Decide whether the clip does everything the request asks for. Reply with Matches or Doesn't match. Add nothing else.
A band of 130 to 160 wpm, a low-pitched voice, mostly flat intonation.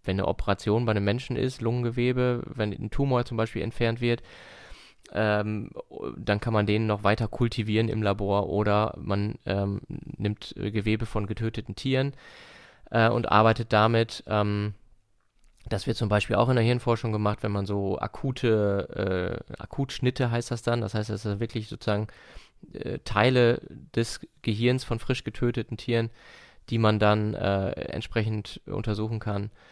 Matches